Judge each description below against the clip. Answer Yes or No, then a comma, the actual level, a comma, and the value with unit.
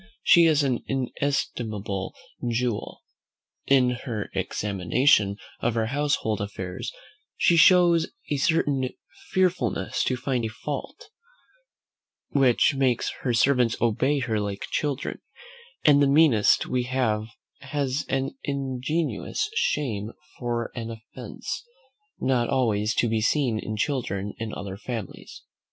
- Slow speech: Yes, slow, 120 wpm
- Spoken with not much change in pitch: No, average, 4.4 semitones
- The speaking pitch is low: Yes, low, 125 Hz